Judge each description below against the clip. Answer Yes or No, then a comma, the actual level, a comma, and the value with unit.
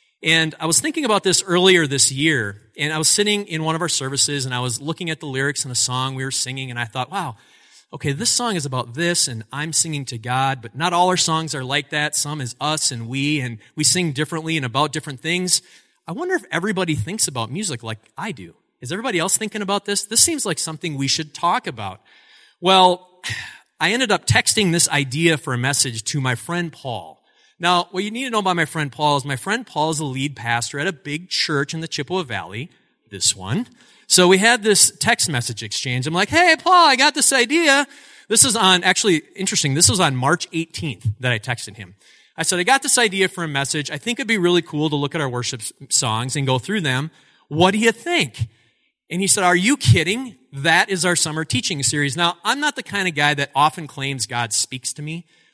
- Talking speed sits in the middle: No, fast, 235 wpm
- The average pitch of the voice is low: No, medium, 155 Hz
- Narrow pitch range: No, wide, 5.6 semitones